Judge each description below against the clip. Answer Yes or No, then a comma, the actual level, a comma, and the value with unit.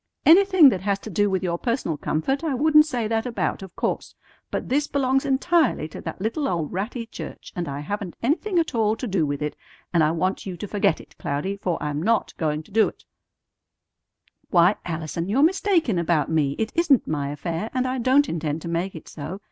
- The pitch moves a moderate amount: No, wide, 7.9 semitones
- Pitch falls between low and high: No, high, 200 Hz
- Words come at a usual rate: No, fast, 210 wpm